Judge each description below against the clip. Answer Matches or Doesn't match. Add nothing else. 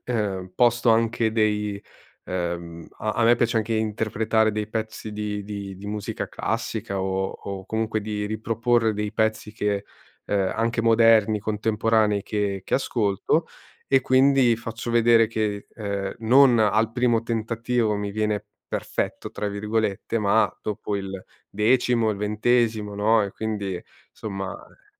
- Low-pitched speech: Matches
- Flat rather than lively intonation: Matches